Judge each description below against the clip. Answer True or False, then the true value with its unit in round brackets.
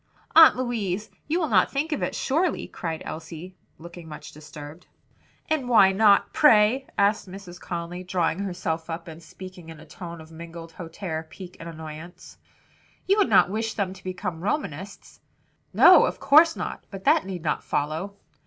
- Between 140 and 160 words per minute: False (170 wpm)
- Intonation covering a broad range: False (4.4 semitones)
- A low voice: False (185 Hz)